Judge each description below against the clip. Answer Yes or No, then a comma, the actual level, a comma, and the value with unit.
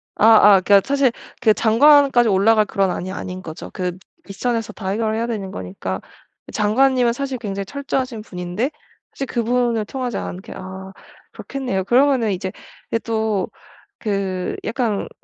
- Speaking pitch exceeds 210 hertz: Yes, high, 220 Hz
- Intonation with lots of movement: No, average, 4.3 semitones